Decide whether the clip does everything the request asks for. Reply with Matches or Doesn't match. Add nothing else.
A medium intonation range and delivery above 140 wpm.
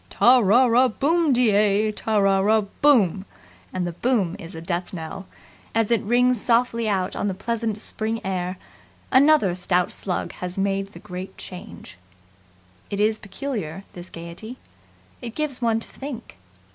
Matches